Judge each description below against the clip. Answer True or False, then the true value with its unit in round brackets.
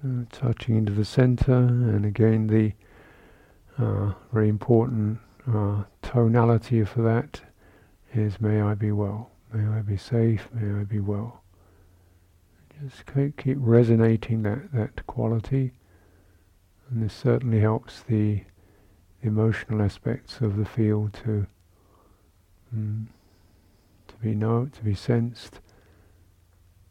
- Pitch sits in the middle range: False (105 Hz)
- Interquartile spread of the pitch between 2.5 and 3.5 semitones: True (2.8 semitones)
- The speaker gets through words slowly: True (115 wpm)